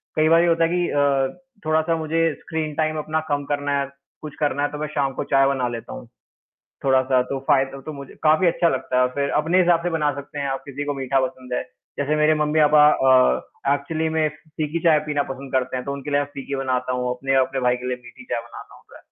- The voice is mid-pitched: Yes, medium, 145 Hz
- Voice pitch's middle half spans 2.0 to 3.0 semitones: Yes, average, 2.7 semitones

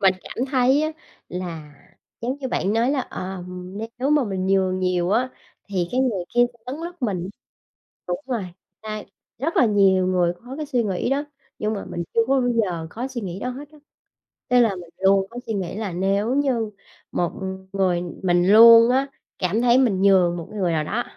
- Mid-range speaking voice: No, high, 210 Hz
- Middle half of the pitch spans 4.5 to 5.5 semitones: Yes, average, 5.2 semitones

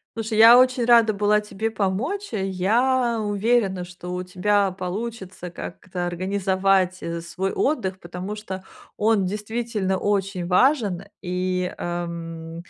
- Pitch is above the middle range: Yes, high, 195 Hz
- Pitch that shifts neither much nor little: Yes, average, 3.4 semitones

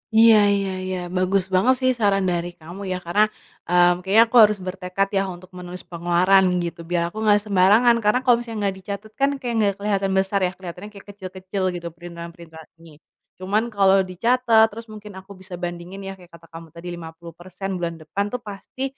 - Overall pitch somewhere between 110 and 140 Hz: No, high, 190 Hz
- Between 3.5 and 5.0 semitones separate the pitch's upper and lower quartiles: No, average, 2.8 semitones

